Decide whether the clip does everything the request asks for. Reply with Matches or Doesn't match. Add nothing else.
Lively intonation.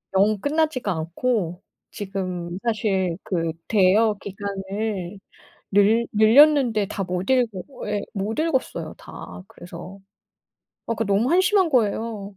Doesn't match